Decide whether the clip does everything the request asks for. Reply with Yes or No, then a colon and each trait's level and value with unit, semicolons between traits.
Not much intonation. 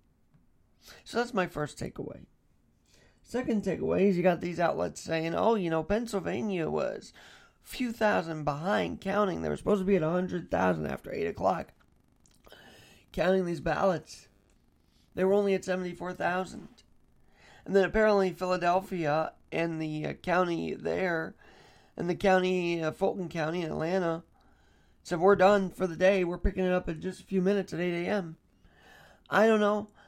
No: average, 3.0 semitones